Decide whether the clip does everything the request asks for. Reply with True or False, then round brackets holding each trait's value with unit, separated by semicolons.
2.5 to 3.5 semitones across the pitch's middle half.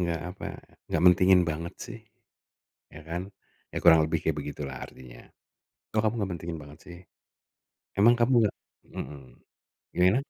False (4.4 semitones)